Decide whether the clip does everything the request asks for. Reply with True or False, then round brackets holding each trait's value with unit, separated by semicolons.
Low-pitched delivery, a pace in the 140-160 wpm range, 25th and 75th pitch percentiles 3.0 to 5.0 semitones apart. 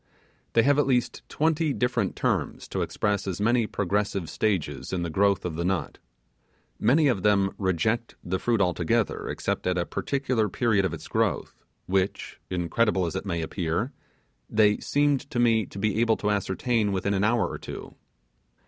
False (105 Hz; 175 wpm; 4.1 semitones)